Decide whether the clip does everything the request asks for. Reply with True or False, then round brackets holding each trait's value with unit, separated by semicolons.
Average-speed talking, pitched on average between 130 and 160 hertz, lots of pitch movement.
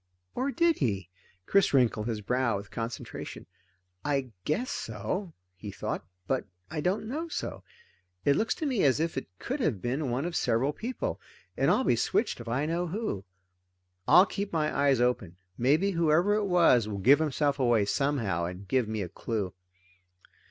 True (175 wpm; 140 Hz; 8.1 semitones)